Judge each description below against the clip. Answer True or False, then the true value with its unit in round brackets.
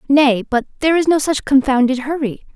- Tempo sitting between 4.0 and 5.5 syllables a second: False (5.8 syllables/s)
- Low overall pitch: False (275 Hz)